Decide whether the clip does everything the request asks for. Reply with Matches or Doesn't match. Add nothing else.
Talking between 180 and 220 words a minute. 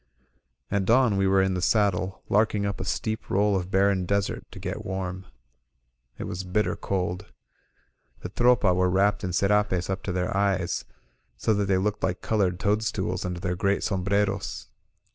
Doesn't match